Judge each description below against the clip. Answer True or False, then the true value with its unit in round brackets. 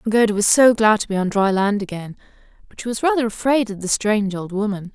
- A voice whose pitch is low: False (210 Hz)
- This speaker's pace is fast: True (255 wpm)